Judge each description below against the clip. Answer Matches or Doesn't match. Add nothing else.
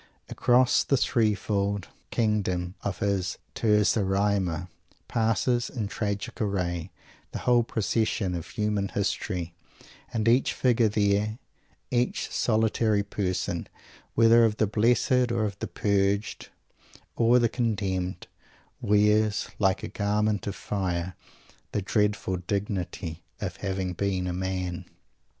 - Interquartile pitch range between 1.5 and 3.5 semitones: Matches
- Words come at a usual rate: Doesn't match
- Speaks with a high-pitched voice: Doesn't match